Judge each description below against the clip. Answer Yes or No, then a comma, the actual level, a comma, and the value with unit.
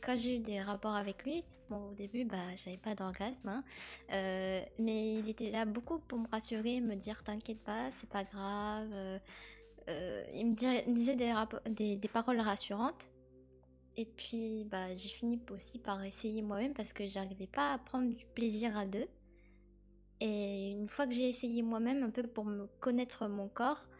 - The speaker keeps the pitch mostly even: No, average, 3.2 semitones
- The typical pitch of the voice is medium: No, high, 220 Hz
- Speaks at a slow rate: No, average, 190 wpm